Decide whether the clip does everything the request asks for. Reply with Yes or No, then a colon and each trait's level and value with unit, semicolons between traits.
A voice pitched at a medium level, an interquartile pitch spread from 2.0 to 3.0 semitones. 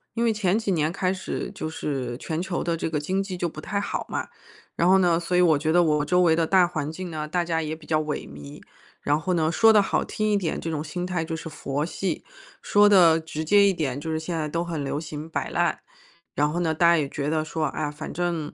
Yes: medium, 165 Hz; average, 2.7 semitones